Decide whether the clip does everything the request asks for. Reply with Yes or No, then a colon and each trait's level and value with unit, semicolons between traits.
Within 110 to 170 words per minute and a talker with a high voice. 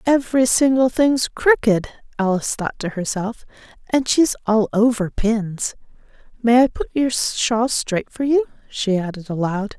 Yes: average, 140 wpm; high, 230 Hz